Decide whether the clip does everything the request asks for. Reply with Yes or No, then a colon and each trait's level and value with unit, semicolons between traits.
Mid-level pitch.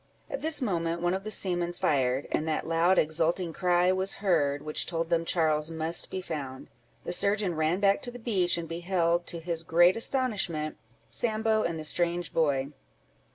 Yes: medium, 170 Hz